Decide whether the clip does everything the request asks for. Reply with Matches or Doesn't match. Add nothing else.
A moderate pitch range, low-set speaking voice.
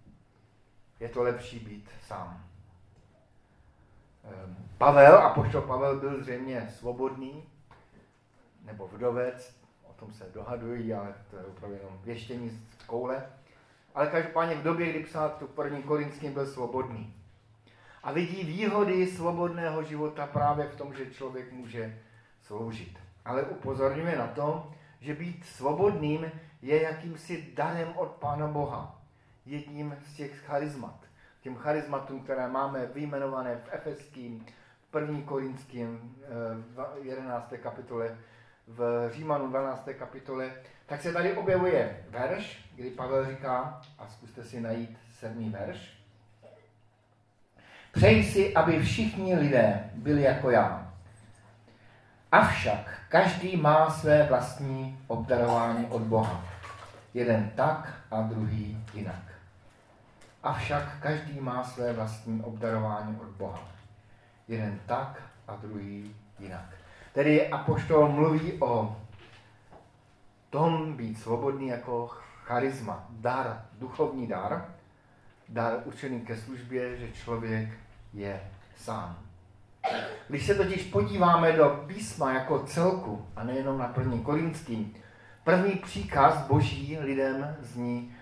Matches